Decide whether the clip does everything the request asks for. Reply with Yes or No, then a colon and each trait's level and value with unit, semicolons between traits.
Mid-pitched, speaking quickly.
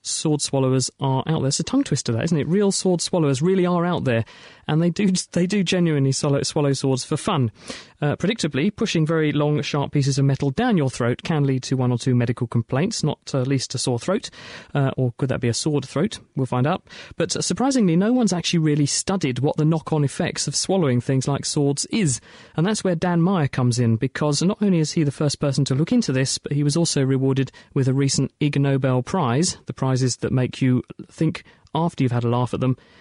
Yes: medium, 145 Hz; fast, 225 wpm